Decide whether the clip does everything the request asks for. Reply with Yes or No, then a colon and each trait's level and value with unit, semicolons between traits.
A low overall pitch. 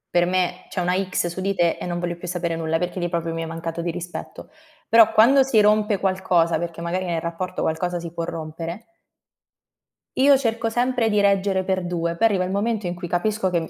No: medium, 180 Hz